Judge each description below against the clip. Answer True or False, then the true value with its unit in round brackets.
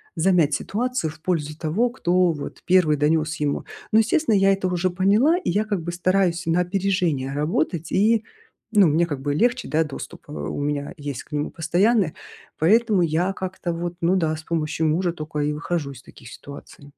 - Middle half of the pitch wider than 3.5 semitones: True (4.0 semitones)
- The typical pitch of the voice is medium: True (170 Hz)